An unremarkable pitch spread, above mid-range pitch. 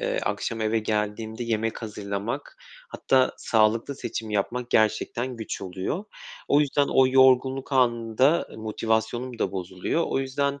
No: average, 3.4 semitones; low, 115 Hz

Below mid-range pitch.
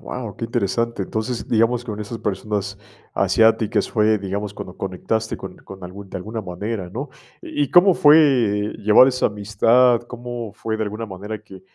Yes: low, 110 Hz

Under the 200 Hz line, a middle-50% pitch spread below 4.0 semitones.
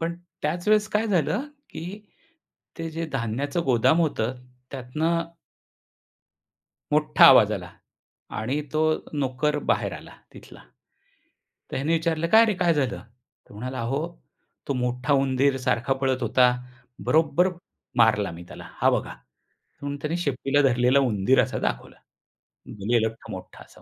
No: medium, 140 Hz; average, 4.8 semitones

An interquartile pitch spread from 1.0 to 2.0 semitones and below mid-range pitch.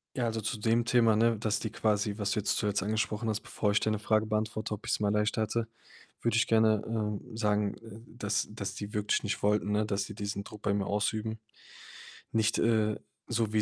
Yes: narrow, 1.3 semitones; low, 110 Hz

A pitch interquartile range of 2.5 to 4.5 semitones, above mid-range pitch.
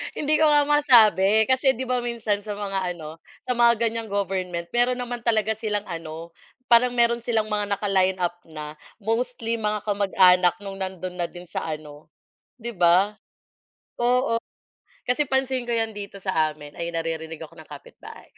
No: average, 5.2 semitones; high, 205 Hz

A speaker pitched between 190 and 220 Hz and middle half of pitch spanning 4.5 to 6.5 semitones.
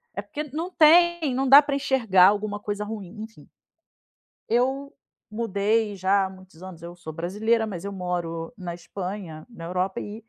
Yes: high, 205 Hz; average, 4.9 semitones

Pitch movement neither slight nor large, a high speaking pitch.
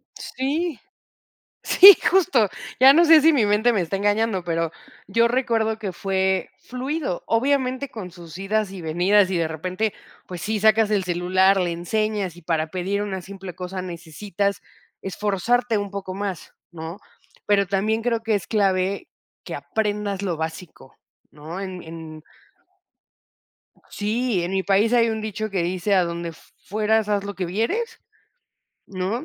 Yes: average, 3.5 semitones; high, 200 Hz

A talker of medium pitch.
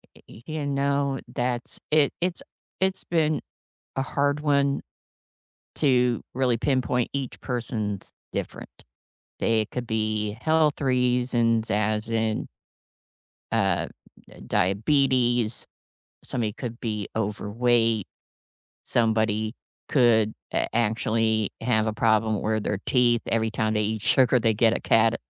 No: low, 115 Hz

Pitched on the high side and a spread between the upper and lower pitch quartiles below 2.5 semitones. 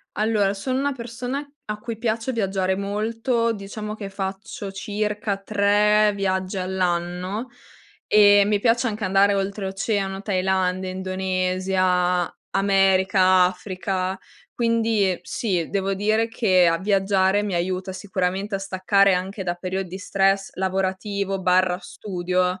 Yes: high, 195 Hz; narrow, 2.0 semitones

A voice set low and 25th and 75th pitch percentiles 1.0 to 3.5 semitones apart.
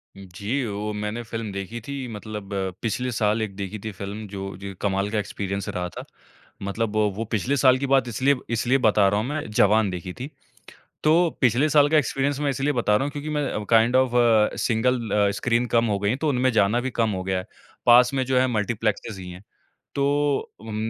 No: low, 115 Hz; average, 4.2 semitones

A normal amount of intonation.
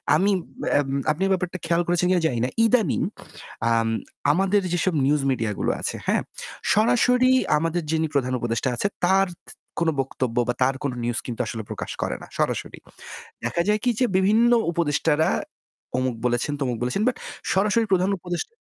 No: wide, 7.1 semitones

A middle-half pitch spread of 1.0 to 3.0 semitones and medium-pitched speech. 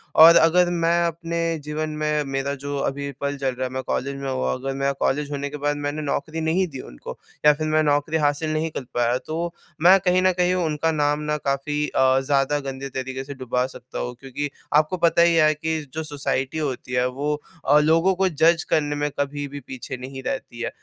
Yes: average, 2.7 semitones; medium, 145 Hz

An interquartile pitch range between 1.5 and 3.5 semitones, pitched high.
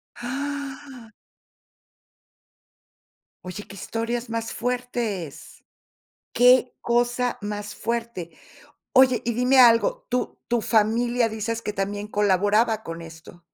Yes: average, 3.0 semitones; high, 230 Hz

